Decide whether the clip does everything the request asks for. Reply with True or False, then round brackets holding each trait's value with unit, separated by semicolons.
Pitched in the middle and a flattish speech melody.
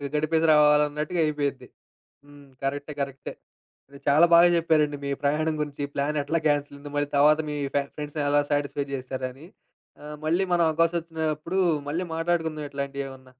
True (150 Hz; 1.9 semitones)